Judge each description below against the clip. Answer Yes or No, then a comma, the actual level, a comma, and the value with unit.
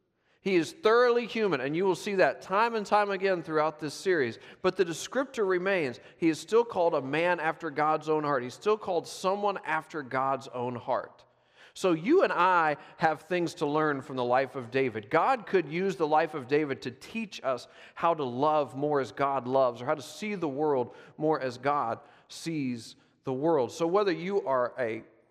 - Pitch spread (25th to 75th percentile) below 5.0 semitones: No, wide, 5.6 semitones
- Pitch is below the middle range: No, medium, 155 Hz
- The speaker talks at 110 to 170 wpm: No, average, 200 wpm